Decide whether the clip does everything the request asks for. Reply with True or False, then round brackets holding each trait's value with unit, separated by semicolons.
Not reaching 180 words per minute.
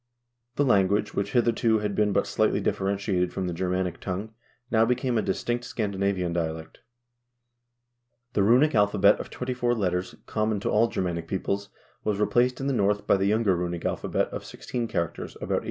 False (185 wpm)